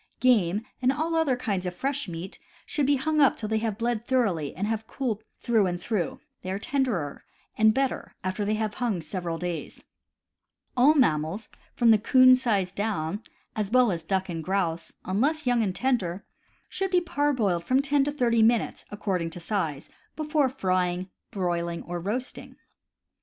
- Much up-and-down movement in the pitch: Yes, wide, 6.0 semitones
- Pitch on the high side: Yes, high, 215 Hz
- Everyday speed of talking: Yes, average, 175 wpm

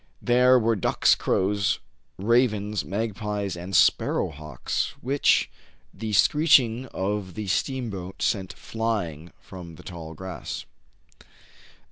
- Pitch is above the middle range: No, low, 105 Hz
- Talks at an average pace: No, slow, 110 wpm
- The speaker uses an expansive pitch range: No, average, 3.7 semitones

